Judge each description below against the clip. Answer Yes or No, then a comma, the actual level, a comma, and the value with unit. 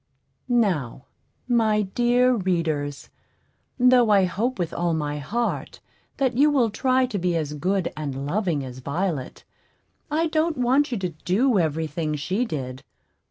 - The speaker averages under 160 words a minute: Yes, average, 150 wpm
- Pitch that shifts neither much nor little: No, wide, 8.1 semitones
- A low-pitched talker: No, high, 190 Hz